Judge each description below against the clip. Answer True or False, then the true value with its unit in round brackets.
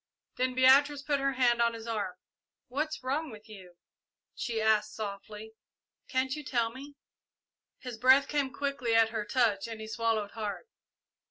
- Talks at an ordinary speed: True (160 wpm)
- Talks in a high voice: True (235 Hz)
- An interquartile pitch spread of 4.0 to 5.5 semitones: False (3.5 semitones)